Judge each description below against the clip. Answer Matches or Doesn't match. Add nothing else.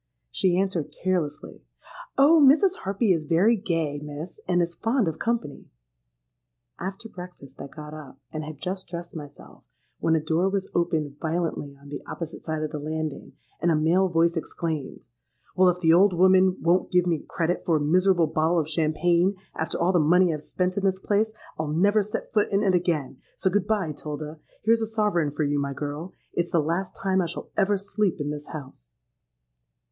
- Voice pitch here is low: Doesn't match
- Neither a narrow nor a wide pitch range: Matches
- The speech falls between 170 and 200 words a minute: Matches